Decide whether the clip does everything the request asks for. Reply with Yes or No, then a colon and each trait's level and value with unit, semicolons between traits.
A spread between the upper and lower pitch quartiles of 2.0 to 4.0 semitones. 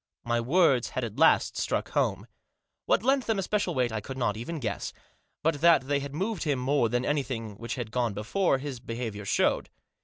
No: average, 5.3 semitones